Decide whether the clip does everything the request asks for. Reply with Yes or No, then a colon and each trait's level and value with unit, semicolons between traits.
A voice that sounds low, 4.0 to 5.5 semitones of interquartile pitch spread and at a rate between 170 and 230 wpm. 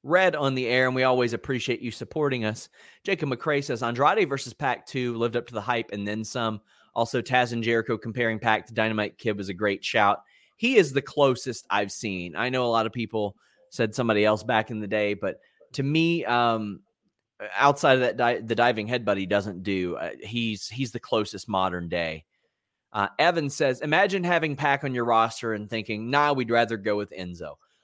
No: low, 115 Hz; average, 3.2 semitones; fast, 205 wpm